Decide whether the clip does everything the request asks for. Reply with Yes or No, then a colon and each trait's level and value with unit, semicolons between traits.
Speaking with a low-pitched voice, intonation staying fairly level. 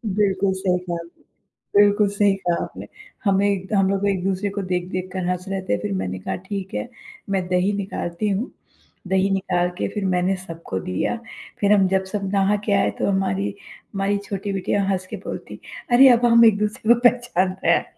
No: high, 195 Hz; narrow, 1.9 semitones